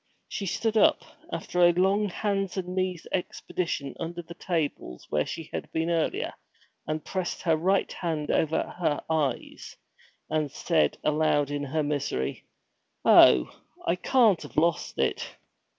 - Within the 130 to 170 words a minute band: Yes, average, 145 wpm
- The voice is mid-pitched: Yes, medium, 165 Hz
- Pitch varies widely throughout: No, average, 3.4 semitones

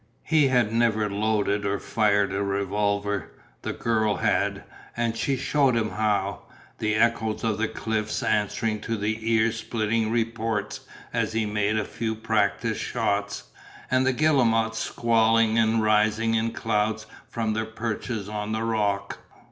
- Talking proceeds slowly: No, average, 150 wpm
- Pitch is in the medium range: No, low, 110 Hz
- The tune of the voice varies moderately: No, narrow, 1.5 semitones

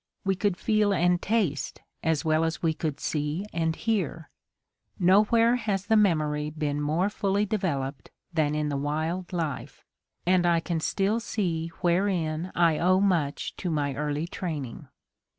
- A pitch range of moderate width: Yes, average, 4.2 semitones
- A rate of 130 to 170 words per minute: Yes, average, 150 wpm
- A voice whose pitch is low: No, medium, 170 Hz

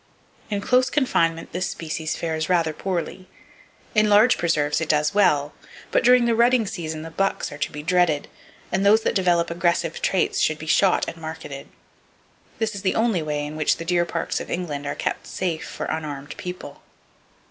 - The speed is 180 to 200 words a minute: Yes, average, 185 wpm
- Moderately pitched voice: Yes, medium, 170 Hz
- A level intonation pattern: No, average, 3.9 semitones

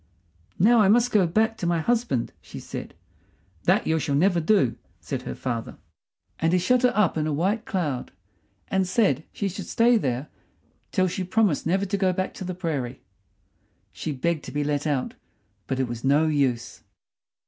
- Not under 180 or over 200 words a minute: Yes, average, 185 wpm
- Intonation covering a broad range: Yes, wide, 5.7 semitones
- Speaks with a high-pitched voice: No, medium, 170 Hz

